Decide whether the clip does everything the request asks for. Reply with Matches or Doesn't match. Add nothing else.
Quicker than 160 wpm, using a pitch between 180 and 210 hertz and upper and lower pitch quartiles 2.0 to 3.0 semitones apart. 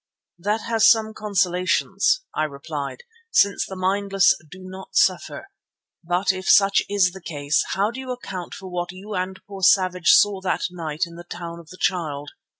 Matches